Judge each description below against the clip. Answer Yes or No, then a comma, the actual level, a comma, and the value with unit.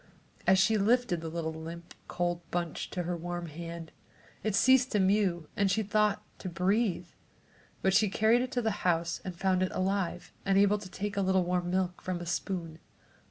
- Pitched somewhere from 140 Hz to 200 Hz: Yes, medium, 185 Hz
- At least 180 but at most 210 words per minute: Yes, average, 195 wpm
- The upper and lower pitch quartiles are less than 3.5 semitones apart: Yes, average, 2.8 semitones